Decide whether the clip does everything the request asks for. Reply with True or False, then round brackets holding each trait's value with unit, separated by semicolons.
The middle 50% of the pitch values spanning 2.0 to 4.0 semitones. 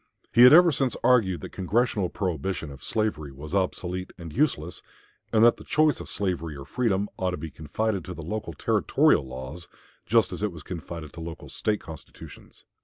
False (5.3 semitones)